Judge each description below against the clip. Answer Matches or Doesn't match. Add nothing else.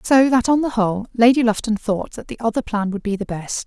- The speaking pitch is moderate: Doesn't match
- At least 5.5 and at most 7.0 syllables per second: Matches